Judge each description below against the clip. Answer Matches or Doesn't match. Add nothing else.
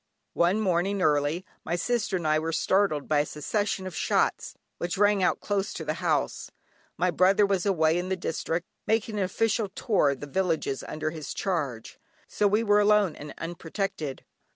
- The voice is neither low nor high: Matches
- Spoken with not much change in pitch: Doesn't match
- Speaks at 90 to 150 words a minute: Doesn't match